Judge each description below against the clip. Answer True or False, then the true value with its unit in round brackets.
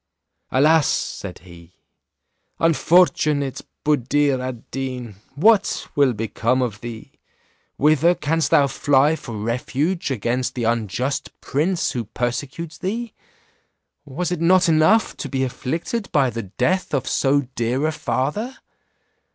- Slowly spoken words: True (125 wpm)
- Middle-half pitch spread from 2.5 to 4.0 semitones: False (4.8 semitones)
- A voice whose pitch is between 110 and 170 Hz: True (140 Hz)